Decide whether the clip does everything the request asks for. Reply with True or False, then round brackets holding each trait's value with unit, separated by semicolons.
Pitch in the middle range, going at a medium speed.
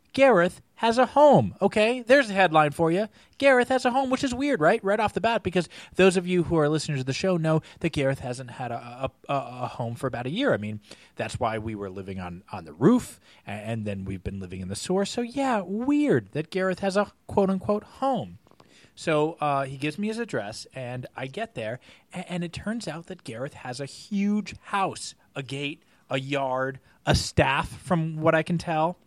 False (160 Hz; 225 wpm)